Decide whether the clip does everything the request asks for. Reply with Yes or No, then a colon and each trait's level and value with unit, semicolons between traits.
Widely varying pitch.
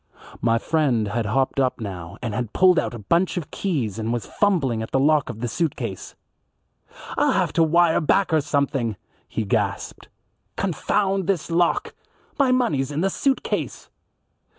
Yes: wide, 7.2 semitones